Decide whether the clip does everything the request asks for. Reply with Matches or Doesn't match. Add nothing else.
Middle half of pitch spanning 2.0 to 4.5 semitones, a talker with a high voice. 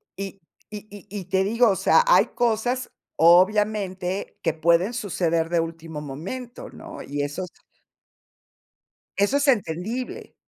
Doesn't match